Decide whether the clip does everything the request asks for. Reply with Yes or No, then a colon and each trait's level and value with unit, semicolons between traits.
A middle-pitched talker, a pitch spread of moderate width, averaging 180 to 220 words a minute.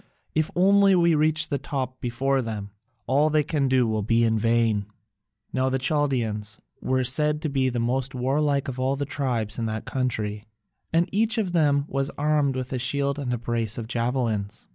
No: low, 130 Hz; average, 3.8 semitones; average, 190 wpm